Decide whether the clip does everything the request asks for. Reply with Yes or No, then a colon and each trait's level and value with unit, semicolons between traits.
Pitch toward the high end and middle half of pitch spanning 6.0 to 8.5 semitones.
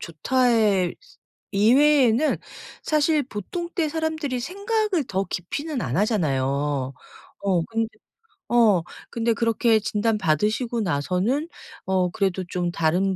Yes: high, 220 Hz; wide, 7.2 semitones